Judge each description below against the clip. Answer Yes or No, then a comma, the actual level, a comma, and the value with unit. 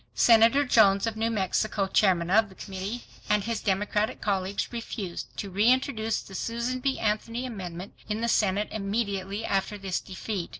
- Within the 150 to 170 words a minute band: Yes, average, 160 wpm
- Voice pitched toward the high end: Yes, high, 210 Hz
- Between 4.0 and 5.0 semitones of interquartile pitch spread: No, average, 2.8 semitones